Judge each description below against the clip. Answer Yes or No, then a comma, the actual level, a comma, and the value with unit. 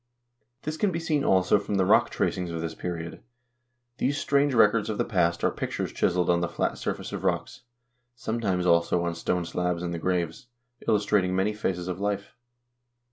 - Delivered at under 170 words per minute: No, average, 190 wpm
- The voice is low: Yes, very low, 95 Hz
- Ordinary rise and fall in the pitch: Yes, average, 3.8 semitones